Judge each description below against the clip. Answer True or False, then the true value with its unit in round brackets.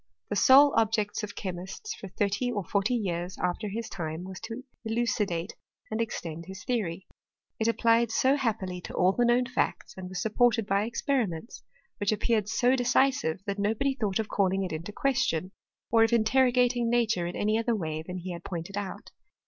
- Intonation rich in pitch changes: False (4.2 semitones)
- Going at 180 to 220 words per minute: True (190 wpm)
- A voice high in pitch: True (210 Hz)